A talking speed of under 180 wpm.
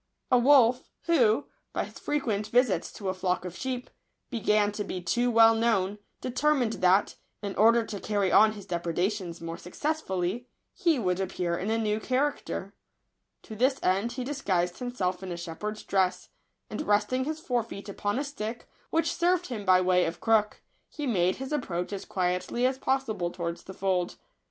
No: average, 185 wpm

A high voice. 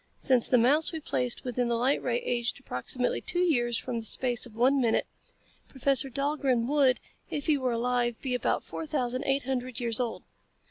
Yes: very high, 250 Hz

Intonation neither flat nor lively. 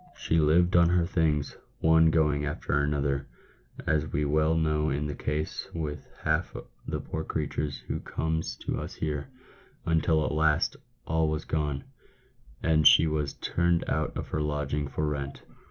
No: narrow, 1.5 semitones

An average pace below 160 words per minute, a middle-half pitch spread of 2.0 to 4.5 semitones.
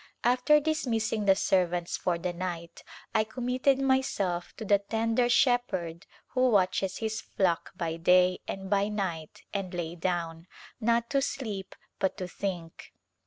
No: average, 150 wpm; average, 5.0 semitones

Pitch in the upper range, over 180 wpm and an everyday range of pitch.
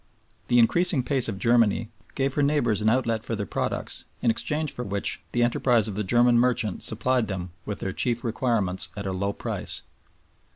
No: low, 115 Hz; average, 190 wpm; average, 3.3 semitones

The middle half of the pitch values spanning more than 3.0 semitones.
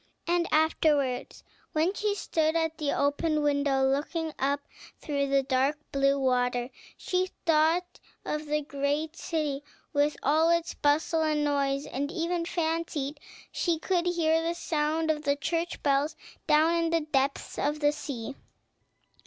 No: narrow, 2.5 semitones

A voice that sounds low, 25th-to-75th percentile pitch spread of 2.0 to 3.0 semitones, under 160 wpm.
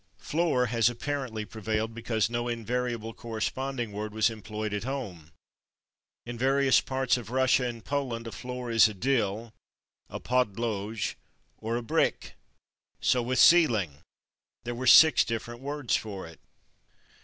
Yes: low, 120 Hz; narrow, 2.6 semitones; average, 140 wpm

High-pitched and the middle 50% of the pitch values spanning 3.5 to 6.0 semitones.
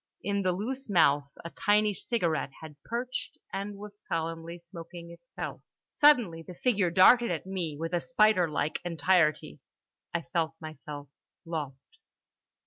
No: medium, 175 Hz; average, 4.2 semitones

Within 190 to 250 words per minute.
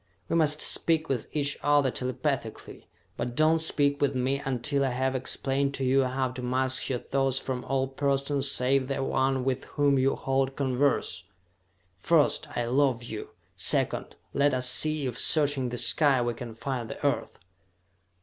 No: average, 170 wpm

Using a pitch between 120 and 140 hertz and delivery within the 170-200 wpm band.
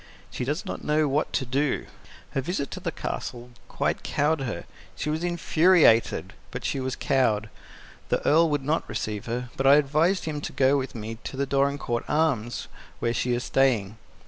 Yes: low, 135 Hz; average, 185 wpm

